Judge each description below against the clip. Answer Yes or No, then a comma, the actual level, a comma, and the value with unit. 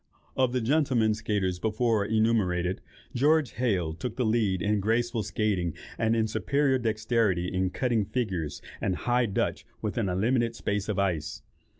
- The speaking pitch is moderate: No, low, 110 Hz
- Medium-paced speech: Yes, average, 155 wpm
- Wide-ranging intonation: No, average, 3.9 semitones